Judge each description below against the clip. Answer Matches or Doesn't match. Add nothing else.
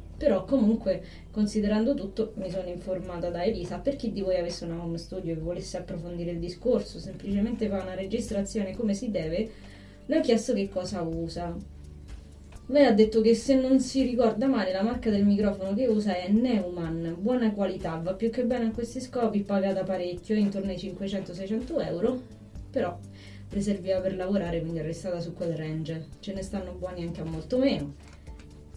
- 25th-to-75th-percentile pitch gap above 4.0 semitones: Matches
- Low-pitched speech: Doesn't match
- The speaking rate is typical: Doesn't match